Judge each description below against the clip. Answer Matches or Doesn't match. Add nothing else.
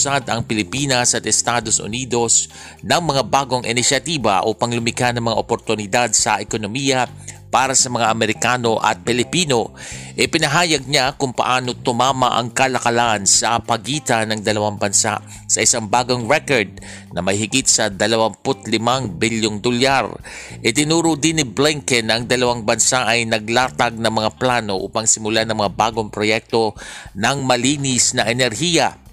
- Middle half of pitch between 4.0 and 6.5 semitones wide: Doesn't match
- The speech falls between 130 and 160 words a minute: Matches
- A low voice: Matches